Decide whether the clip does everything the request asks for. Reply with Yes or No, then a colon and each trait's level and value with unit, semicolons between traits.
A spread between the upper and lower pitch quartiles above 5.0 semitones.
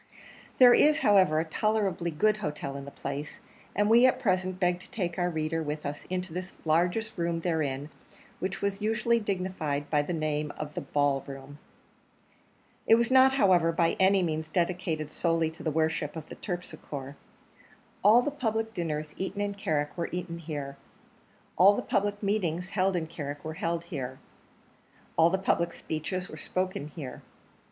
No: average, 4.2 semitones